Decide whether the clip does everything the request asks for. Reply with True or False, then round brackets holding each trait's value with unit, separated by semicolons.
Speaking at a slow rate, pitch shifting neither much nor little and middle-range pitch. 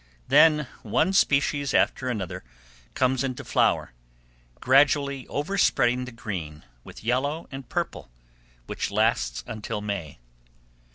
False (110 wpm; 4.5 semitones; 125 Hz)